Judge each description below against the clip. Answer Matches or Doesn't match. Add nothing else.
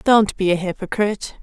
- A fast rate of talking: Doesn't match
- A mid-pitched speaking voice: Doesn't match